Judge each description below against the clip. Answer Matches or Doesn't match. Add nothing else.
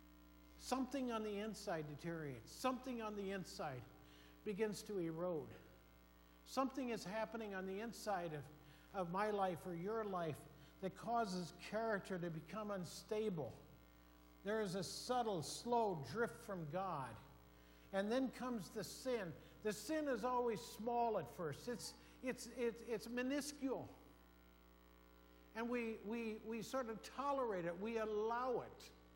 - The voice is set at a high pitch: Matches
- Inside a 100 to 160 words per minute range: Matches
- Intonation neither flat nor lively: Doesn't match